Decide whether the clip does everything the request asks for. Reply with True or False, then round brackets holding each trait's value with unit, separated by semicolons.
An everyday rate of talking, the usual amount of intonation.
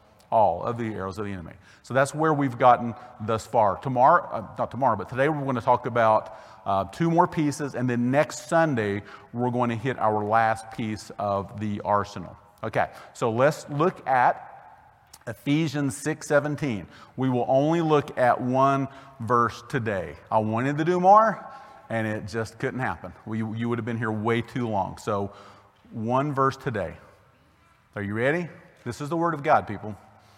True (180 wpm; 4.5 semitones)